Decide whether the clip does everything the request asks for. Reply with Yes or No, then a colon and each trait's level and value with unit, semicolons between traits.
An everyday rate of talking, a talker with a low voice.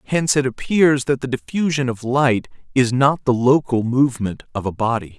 Yes: average, 185 wpm; low, 125 Hz